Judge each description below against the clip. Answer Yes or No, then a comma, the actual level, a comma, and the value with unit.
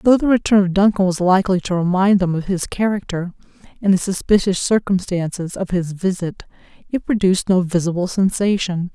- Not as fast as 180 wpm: Yes, average, 170 wpm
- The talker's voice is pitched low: No, high, 190 Hz